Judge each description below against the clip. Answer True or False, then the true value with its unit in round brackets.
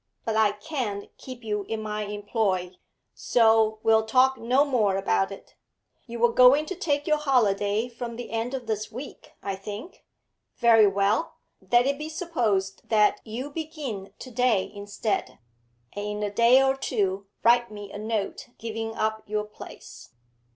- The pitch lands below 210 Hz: False (225 Hz)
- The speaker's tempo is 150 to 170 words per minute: True (165 wpm)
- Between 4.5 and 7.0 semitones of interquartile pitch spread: False (3.5 semitones)